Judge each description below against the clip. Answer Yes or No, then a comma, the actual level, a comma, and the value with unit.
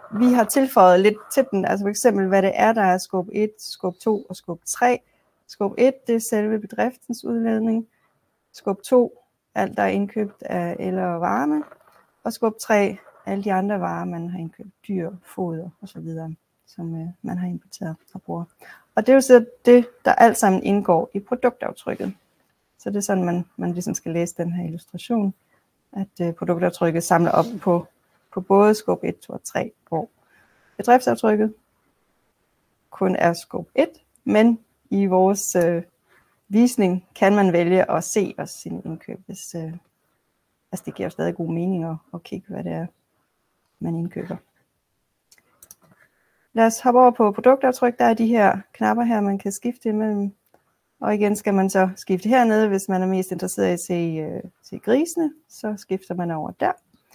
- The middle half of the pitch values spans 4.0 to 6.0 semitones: Yes, average, 4.3 semitones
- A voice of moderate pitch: No, high, 200 Hz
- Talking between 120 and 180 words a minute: Yes, average, 175 wpm